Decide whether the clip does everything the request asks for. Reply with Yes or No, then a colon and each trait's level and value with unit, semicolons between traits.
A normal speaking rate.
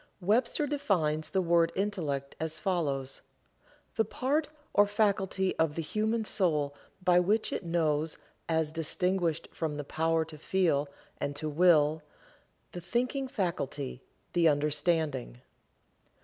No: slow, 125 wpm